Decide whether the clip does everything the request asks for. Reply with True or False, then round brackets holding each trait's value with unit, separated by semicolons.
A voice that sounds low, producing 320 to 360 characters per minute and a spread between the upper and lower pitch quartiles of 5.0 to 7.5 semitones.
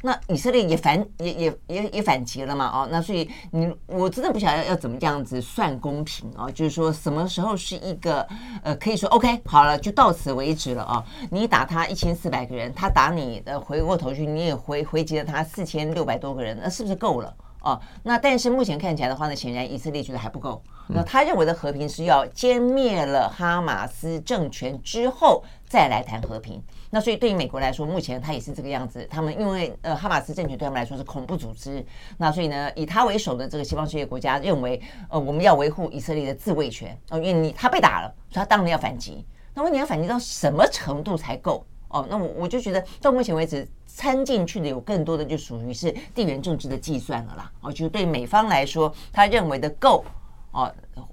False (160 Hz; 345 characters per minute; 5.6 semitones)